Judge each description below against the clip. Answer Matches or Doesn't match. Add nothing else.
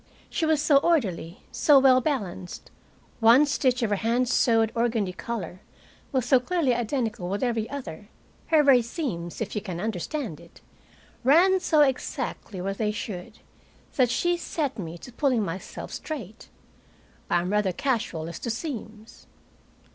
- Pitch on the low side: Doesn't match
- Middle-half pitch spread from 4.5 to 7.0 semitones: Matches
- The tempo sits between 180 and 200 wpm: Doesn't match